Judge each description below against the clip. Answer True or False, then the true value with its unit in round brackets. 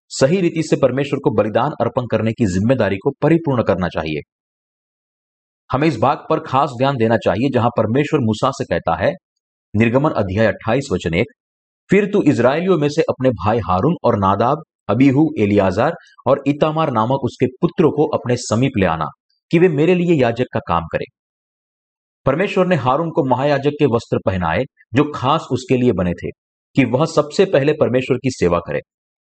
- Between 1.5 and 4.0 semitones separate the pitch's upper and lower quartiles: False (5.4 semitones)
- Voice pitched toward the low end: True (130 Hz)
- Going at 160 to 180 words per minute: True (175 wpm)